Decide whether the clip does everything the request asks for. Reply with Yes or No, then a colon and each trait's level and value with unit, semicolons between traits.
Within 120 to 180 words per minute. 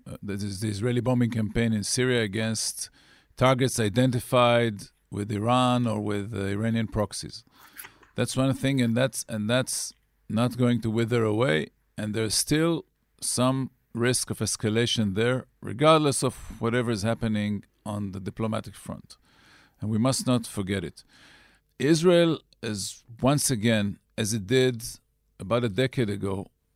Yes: average, 145 wpm